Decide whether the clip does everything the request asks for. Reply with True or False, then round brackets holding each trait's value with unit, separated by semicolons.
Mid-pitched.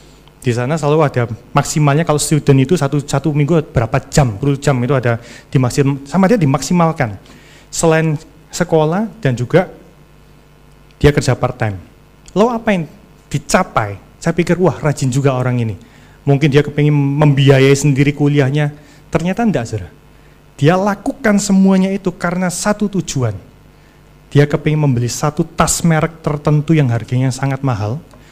True (150 Hz)